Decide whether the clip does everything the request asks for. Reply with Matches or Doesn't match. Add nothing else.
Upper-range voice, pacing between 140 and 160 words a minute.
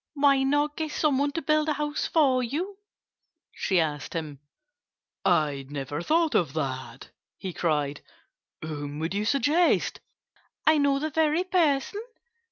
Matches